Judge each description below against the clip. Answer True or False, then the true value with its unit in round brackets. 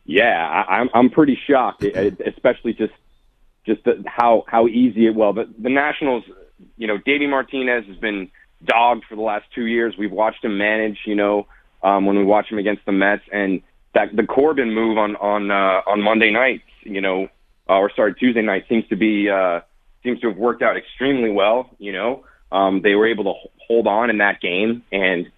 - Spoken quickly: True (210 wpm)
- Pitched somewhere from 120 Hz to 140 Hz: False (110 Hz)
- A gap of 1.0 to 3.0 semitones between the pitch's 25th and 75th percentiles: True (2.5 semitones)